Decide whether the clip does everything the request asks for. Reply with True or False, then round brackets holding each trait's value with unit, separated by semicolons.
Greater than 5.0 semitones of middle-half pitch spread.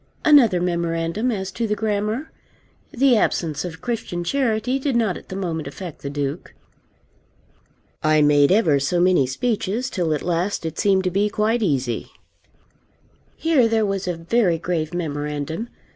True (5.4 semitones)